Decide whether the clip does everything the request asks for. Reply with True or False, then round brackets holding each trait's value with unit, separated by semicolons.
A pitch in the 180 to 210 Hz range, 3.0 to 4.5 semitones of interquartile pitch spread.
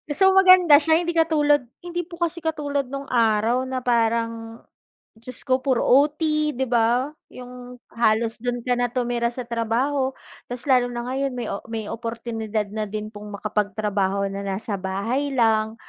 False (245 Hz; 3.6 semitones)